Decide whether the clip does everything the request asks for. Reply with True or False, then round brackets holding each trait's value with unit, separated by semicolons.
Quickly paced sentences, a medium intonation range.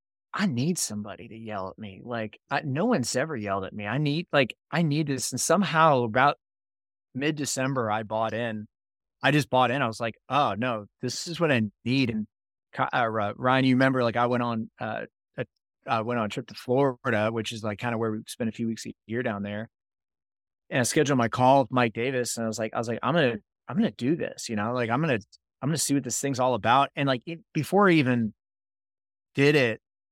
True (235 wpm; 4.1 semitones)